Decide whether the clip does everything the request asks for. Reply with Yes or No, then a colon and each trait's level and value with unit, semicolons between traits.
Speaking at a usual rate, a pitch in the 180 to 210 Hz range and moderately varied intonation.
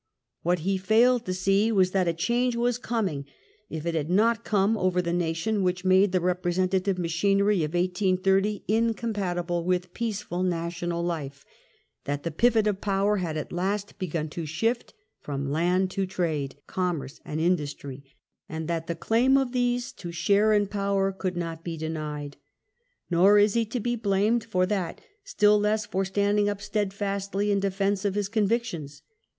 Yes: average, 170 wpm; high, 190 Hz; average, 3.5 semitones